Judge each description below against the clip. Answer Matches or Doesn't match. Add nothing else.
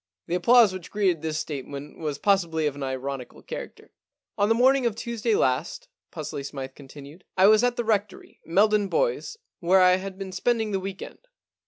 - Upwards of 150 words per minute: Matches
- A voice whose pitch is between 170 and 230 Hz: Matches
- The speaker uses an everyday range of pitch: Doesn't match